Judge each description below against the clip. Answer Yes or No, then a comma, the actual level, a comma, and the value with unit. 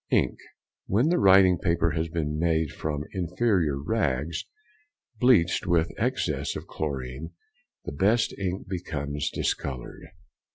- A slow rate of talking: Yes, slow, 115 wpm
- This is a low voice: Yes, very low, 85 Hz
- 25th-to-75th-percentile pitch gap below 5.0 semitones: Yes, average, 4.2 semitones